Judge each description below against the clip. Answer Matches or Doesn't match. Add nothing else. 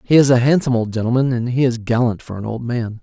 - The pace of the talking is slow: Doesn't match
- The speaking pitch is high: Doesn't match